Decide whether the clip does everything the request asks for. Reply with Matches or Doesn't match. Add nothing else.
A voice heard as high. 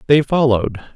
Doesn't match